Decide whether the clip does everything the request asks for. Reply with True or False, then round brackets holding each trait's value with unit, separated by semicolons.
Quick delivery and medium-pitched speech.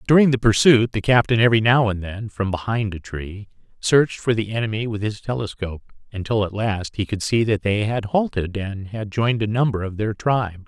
False (215 wpm; 110 Hz)